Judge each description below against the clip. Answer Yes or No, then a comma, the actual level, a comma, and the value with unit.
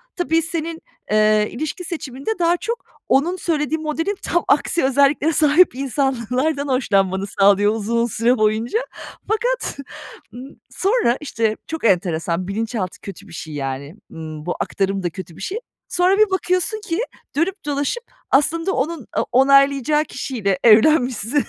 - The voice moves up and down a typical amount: No, wide, 7.7 semitones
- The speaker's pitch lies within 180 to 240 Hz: No, very high, 270 Hz